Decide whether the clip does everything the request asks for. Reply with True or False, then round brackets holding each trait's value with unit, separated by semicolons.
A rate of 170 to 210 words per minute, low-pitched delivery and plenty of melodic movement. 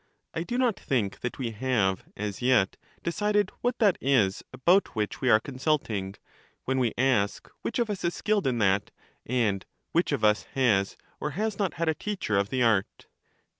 True (195 wpm; 130 Hz; 8.5 semitones)